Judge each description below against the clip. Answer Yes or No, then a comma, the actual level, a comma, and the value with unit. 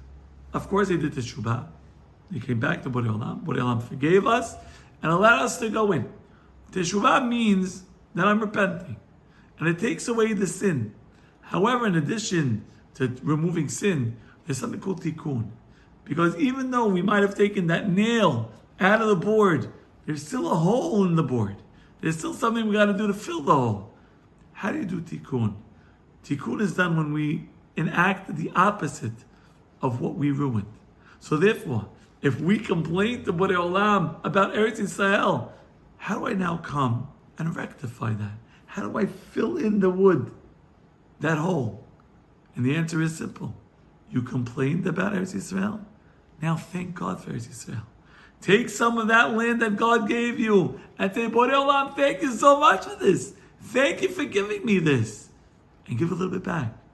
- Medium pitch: Yes, medium, 180 Hz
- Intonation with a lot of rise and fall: Yes, wide, 7.6 semitones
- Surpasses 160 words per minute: Yes, average, 170 wpm